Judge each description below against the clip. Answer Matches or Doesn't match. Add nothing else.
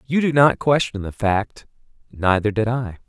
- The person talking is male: Matches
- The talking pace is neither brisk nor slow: Matches